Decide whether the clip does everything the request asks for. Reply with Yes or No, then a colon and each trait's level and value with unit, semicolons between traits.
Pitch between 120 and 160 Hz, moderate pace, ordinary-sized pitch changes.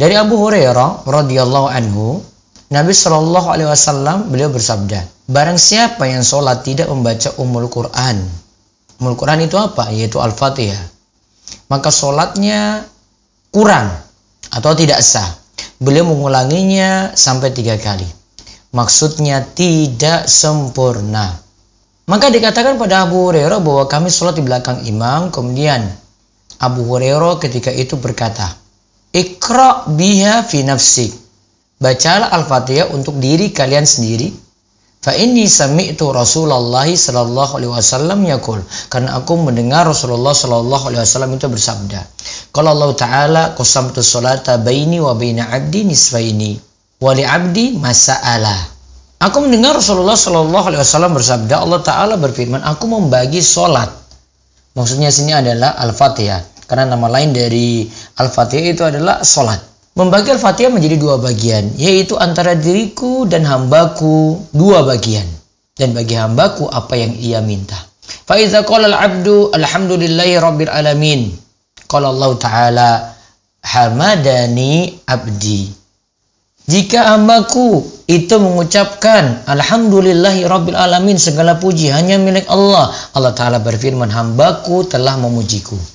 No: low, 135 Hz; average, 115 wpm; wide, 6.8 semitones